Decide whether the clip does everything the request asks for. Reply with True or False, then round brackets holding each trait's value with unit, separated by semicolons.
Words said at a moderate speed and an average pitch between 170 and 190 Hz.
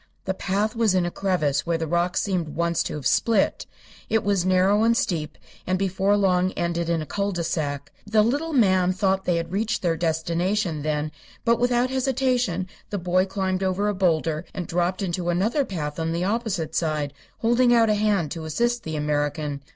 True (195 wpm; 185 Hz)